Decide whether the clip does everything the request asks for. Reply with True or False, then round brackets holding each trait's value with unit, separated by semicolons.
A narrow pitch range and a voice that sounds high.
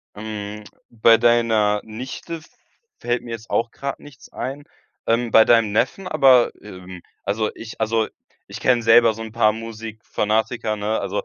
False (1.7 semitones; 115 Hz)